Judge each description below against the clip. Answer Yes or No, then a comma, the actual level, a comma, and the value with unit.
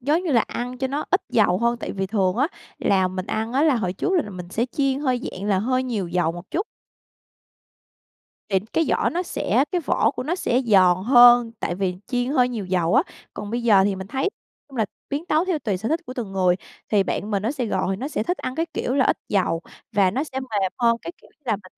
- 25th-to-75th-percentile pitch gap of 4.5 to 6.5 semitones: Yes, wide, 5.6 semitones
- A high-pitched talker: Yes, high, 235 Hz